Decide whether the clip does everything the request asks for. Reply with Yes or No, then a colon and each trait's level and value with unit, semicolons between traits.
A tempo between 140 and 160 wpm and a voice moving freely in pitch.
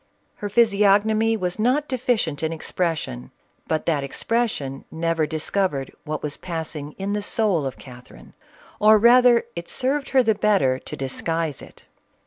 Yes: average, 145 wpm; wide, 6.4 semitones